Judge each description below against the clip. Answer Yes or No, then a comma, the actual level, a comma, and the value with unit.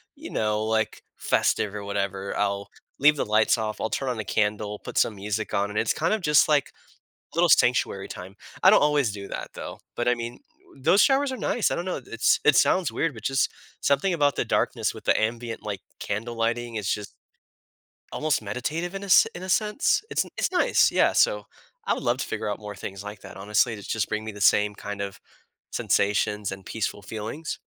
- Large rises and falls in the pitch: Yes, wide, 5.9 semitones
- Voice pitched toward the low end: Yes, low, 110 Hz